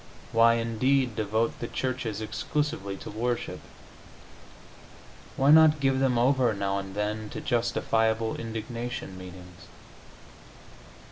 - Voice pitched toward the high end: No, low, 115 Hz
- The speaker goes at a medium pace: No, slow, 110 wpm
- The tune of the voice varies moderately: Yes, average, 3.1 semitones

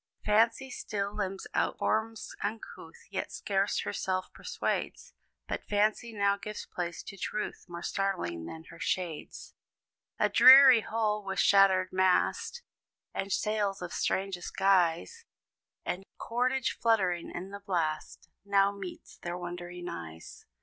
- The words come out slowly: Yes, slow, 130 wpm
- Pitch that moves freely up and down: No, average, 3.1 semitones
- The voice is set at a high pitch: Yes, high, 195 Hz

